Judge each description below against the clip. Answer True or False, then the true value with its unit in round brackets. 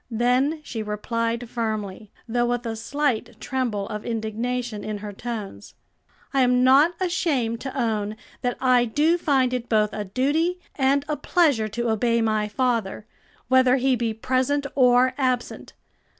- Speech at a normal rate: True (150 wpm)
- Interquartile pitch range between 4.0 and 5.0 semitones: False (3.1 semitones)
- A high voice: True (245 Hz)